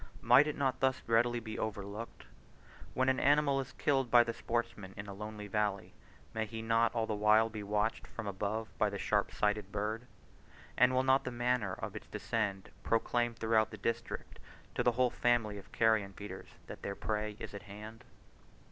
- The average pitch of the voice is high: No, low, 110 Hz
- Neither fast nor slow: Yes, average, 190 wpm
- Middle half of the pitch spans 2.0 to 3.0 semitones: Yes, narrow, 2.5 semitones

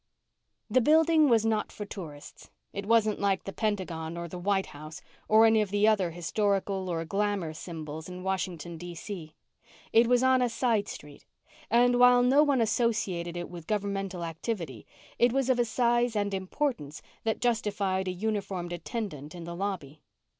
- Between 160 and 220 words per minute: Yes, average, 170 wpm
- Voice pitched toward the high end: Yes, high, 200 Hz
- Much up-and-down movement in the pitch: No, average, 4.8 semitones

